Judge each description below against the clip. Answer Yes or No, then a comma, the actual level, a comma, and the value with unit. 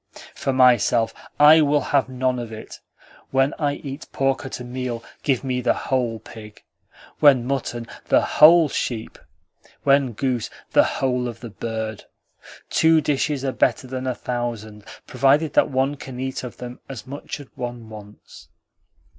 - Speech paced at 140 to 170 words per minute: Yes, average, 160 wpm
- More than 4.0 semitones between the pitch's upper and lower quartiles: No, narrow, 2.6 semitones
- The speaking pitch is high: No, low, 130 Hz